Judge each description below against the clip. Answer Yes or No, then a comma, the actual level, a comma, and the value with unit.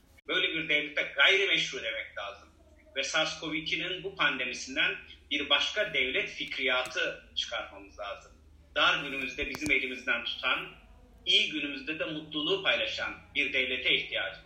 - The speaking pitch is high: No, medium, 160 Hz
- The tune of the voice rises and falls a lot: Yes, wide, 6.8 semitones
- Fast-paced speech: No, average, 120 wpm